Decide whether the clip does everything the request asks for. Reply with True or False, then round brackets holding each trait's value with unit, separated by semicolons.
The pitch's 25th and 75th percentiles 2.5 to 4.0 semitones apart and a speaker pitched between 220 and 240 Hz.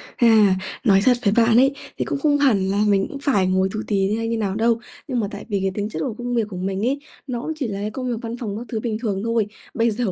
True (3.4 semitones; 225 Hz)